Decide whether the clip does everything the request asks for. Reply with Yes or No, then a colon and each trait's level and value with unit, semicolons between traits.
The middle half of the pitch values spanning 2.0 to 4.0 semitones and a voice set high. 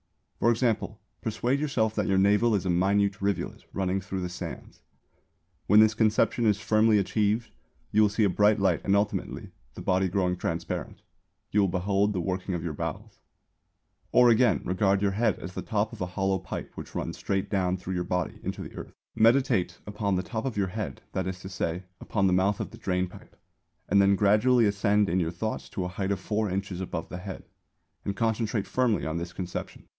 No: average, 2.7 semitones; low, 100 Hz